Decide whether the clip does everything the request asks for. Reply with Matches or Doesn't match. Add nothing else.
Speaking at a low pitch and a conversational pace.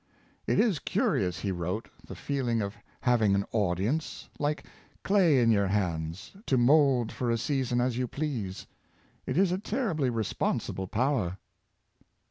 Matches